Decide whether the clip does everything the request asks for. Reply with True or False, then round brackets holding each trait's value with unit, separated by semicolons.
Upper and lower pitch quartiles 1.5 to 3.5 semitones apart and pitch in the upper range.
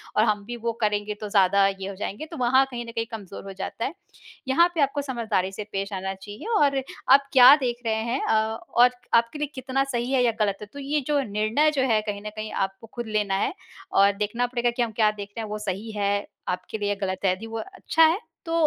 False (4.2 semitones; 225 Hz)